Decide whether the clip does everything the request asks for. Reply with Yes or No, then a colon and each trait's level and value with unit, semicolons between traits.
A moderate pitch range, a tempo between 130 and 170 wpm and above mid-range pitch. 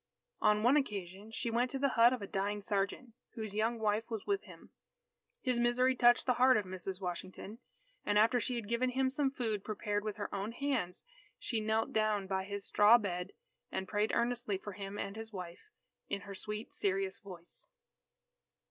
No: average, 3.3 semitones; average, 190 wpm; high, 215 Hz